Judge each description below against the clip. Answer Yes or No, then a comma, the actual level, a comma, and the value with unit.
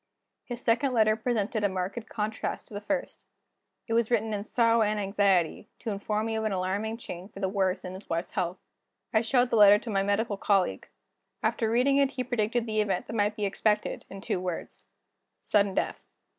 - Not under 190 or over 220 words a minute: Yes, average, 200 wpm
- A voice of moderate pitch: No, high, 210 Hz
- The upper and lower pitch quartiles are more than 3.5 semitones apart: No, narrow, 2.6 semitones